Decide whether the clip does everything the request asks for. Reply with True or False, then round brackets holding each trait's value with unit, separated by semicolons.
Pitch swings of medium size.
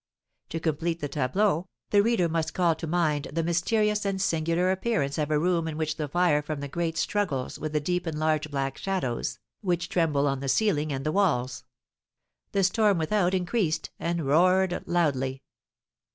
True (3.6 semitones)